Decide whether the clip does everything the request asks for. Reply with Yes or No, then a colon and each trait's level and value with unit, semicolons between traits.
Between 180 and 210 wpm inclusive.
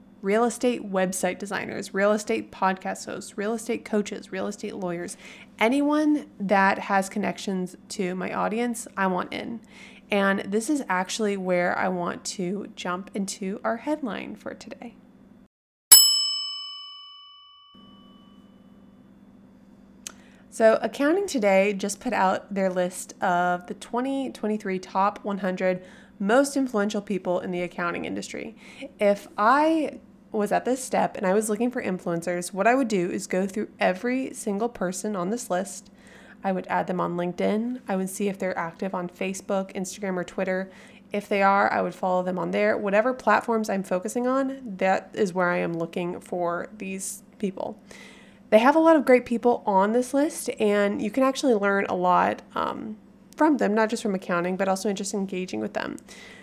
No: average, 165 wpm